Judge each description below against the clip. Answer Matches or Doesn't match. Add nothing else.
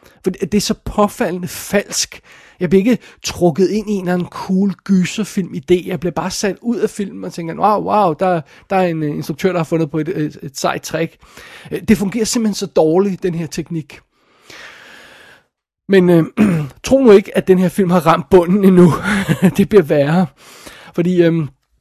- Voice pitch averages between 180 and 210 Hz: Matches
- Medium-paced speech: Matches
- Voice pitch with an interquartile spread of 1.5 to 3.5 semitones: Matches